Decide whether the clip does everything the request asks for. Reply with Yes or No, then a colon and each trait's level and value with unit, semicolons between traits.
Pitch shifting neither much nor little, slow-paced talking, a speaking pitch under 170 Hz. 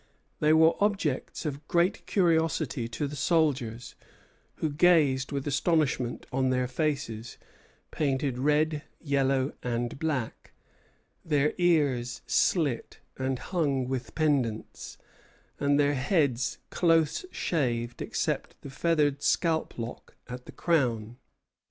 Yes: average, 3.8 semitones; slow, 115 wpm; medium, 140 Hz